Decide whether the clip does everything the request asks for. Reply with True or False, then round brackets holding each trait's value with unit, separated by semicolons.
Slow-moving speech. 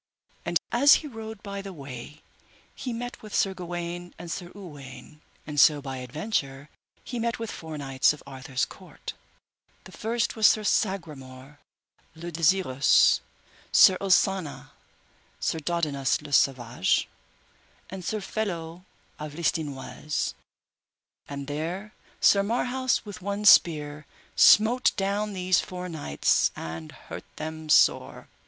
True (130 wpm)